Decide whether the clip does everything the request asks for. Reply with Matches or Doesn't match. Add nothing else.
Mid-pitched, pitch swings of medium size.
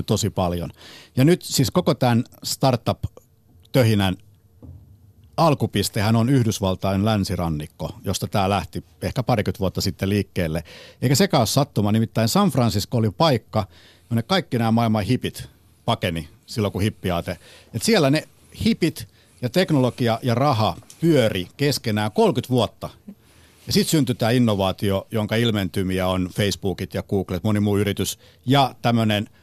Doesn't match